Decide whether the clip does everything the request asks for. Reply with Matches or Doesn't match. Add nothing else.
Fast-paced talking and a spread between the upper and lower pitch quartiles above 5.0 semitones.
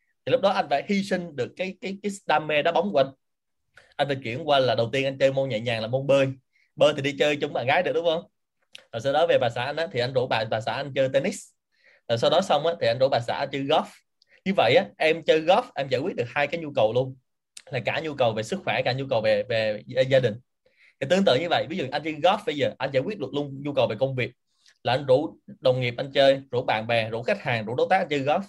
Doesn't match